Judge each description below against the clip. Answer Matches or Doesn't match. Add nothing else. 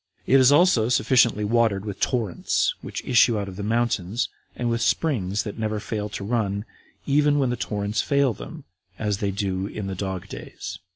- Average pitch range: Matches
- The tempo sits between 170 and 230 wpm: Matches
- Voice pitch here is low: Matches